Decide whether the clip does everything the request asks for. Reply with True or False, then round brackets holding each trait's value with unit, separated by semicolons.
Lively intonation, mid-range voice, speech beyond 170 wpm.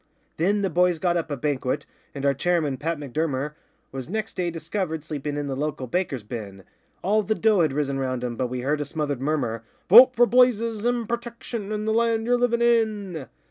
True (7.7 semitones; 165 Hz; 205 wpm)